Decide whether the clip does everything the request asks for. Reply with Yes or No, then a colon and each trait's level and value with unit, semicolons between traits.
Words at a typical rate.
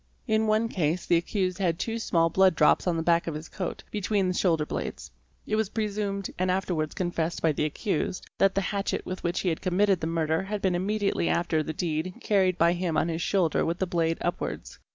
No: fast, 220 wpm